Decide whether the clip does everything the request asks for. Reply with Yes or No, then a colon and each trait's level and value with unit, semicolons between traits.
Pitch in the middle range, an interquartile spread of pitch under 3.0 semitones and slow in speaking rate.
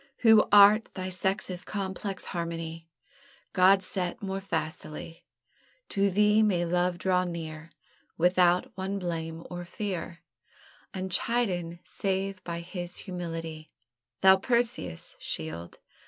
Yes: medium, 180 Hz; narrow, 2.6 semitones; slow, 110 wpm